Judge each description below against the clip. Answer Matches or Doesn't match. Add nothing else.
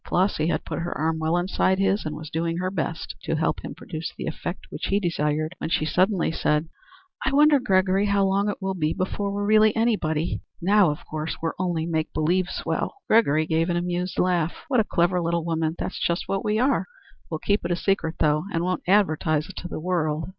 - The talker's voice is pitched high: Doesn't match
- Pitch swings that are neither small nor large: Matches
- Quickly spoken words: Matches